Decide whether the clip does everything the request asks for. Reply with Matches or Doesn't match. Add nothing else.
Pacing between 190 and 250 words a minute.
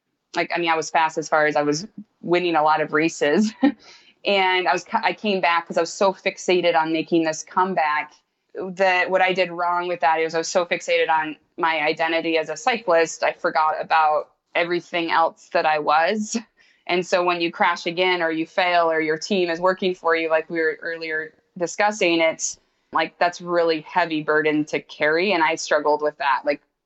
Matches